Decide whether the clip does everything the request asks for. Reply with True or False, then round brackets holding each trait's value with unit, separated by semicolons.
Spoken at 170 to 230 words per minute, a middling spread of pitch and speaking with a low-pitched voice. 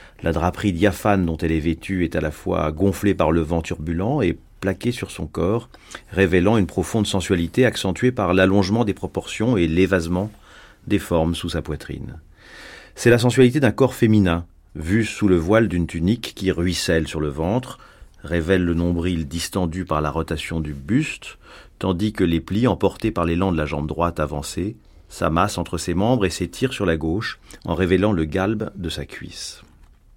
True (180 wpm; 3.8 semitones; 90 Hz)